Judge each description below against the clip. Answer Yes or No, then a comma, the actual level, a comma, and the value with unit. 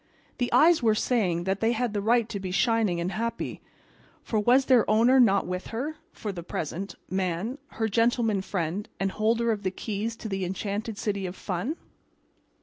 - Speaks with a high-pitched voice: Yes, high, 215 Hz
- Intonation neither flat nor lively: Yes, average, 3.5 semitones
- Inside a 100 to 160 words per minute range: No, average, 185 wpm